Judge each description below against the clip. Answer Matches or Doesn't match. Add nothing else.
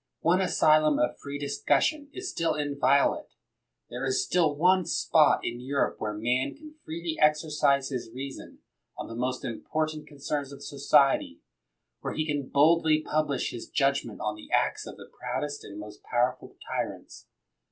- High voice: Doesn't match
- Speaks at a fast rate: Doesn't match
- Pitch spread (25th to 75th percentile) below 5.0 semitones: Matches